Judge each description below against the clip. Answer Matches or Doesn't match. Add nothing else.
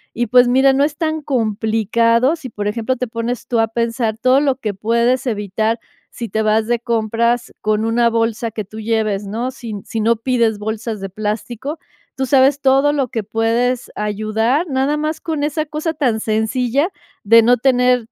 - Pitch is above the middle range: Matches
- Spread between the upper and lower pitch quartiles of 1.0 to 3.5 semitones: Matches